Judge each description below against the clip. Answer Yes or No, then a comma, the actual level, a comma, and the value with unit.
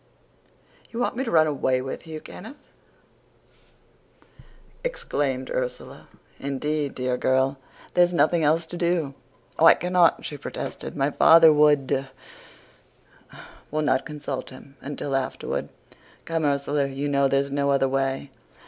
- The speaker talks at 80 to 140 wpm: Yes, slow, 135 wpm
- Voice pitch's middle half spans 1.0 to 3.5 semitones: Yes, average, 3.0 semitones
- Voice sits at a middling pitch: Yes, medium, 145 Hz